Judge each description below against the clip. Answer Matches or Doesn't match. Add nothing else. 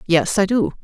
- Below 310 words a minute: Matches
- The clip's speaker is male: Doesn't match